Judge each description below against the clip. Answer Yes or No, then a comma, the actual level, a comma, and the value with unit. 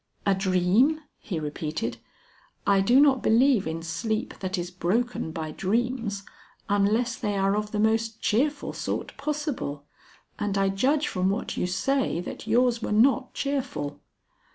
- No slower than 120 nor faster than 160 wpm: Yes, average, 150 wpm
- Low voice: No, high, 210 Hz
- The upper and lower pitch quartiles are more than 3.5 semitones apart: Yes, average, 5.2 semitones